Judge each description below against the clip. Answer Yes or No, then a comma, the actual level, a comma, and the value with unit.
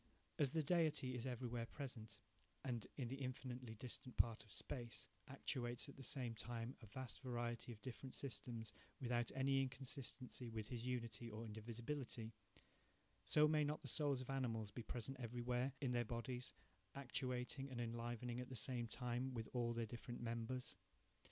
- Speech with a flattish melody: Yes, narrow, 2.1 semitones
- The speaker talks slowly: No, average, 165 wpm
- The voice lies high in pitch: No, low, 125 Hz